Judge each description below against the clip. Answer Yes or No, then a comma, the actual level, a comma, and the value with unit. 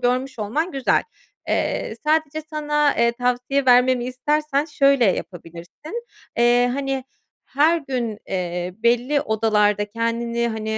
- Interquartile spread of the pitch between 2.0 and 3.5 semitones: No, average, 4.0 semitones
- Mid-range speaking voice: No, high, 245 Hz